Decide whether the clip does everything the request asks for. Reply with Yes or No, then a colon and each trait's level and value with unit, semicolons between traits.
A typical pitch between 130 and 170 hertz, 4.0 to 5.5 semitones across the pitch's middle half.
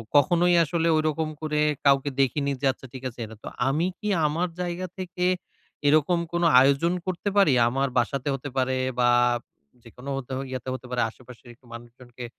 Yes: medium, 140 Hz; average, 4.6 semitones